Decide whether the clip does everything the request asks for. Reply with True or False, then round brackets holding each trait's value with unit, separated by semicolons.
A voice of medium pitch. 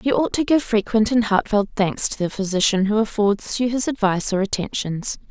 False (215 Hz)